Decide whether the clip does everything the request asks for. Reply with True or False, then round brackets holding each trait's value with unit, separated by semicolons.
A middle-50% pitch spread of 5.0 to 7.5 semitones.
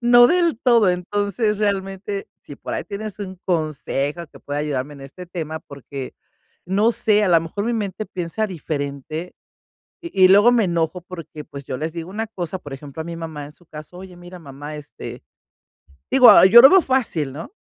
True (5.3 semitones)